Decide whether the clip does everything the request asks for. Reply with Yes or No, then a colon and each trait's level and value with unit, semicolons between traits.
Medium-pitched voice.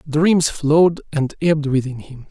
Yes: medium, 150 Hz